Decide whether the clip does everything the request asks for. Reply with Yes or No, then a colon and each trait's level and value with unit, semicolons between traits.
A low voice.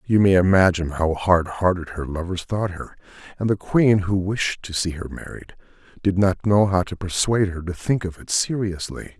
Yes: very low, 95 Hz